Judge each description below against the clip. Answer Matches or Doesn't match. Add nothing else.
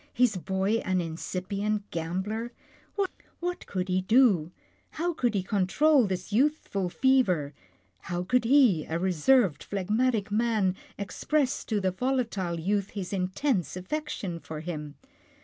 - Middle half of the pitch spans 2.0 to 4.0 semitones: Doesn't match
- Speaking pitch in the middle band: Doesn't match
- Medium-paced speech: Doesn't match